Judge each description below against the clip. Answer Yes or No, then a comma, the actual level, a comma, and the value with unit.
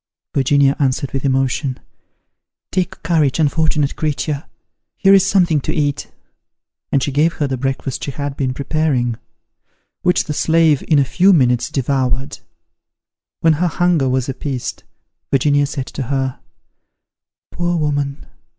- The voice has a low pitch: No, medium, 145 Hz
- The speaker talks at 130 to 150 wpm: Yes, slow, 135 wpm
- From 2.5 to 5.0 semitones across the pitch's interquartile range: Yes, average, 2.9 semitones